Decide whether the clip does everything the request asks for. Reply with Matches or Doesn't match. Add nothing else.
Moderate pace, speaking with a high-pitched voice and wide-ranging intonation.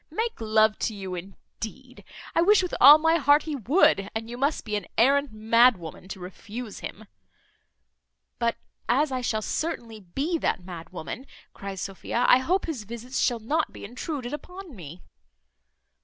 Matches